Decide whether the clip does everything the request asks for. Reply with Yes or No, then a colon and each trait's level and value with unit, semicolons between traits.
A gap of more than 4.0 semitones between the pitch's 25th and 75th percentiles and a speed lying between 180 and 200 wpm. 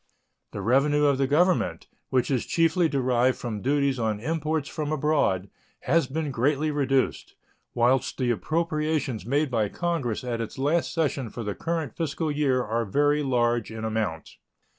No: average, 4.4 semitones; average, 160 wpm